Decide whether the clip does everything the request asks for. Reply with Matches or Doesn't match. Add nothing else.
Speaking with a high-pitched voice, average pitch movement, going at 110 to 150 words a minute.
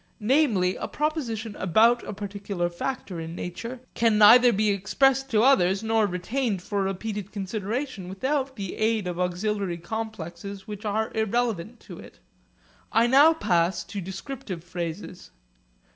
Matches